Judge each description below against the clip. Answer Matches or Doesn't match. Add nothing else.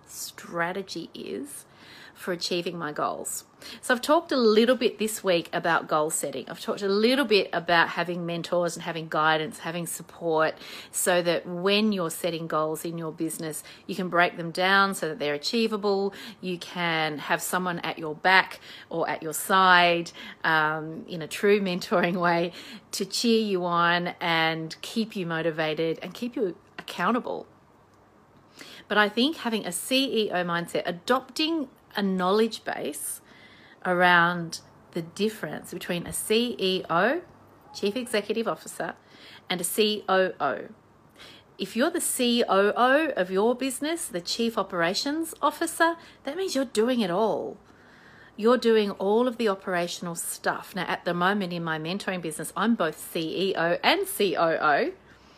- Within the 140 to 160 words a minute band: Matches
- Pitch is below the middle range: Doesn't match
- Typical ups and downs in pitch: Matches